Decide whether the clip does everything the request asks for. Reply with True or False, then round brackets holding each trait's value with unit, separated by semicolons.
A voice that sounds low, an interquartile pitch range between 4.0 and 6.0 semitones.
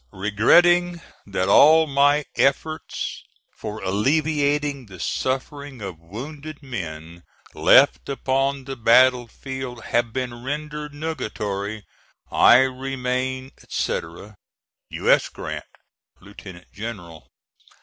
True (130 Hz; 5.5 semitones)